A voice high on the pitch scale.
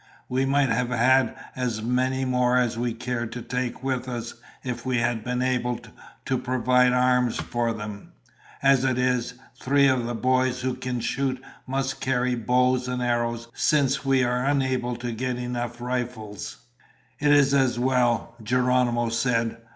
No: low, 125 Hz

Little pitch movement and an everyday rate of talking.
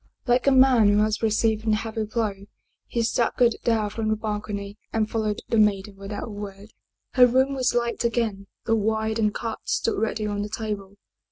Yes: narrow, 1.8 semitones; average, 190 wpm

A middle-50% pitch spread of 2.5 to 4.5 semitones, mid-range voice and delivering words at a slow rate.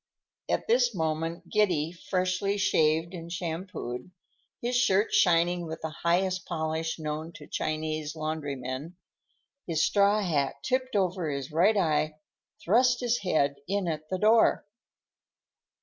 Yes: average, 4.1 semitones; medium, 170 Hz; slow, 130 wpm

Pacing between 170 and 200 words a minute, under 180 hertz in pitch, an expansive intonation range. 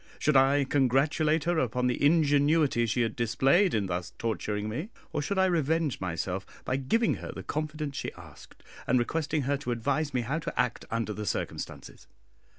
No: average, 180 wpm; low, 135 Hz; average, 4.7 semitones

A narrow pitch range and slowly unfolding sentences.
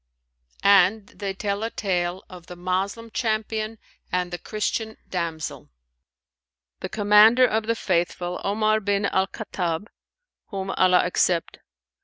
No: average, 3.2 semitones; slow, 125 wpm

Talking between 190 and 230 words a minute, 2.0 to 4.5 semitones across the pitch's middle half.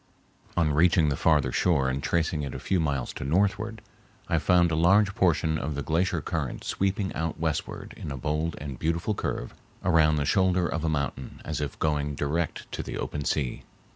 Yes: average, 195 wpm; average, 3.2 semitones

